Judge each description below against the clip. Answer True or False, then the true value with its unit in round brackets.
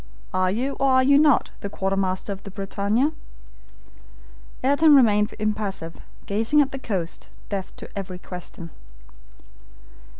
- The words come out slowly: True (130 wpm)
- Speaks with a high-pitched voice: True (205 Hz)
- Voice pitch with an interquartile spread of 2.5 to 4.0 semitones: False (5.5 semitones)